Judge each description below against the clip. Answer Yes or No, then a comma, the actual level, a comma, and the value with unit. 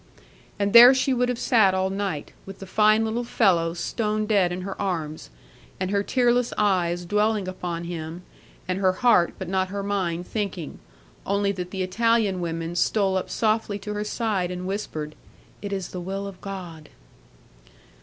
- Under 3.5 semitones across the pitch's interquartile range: Yes, average, 2.9 semitones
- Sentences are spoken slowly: No, average, 175 wpm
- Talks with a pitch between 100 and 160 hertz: No, high, 195 Hz